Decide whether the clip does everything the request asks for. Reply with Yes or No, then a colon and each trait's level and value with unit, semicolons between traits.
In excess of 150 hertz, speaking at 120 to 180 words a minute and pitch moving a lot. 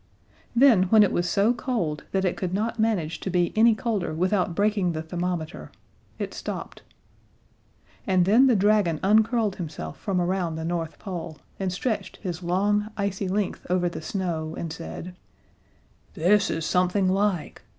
No: medium, 185 Hz; average, 160 wpm; average, 3.3 semitones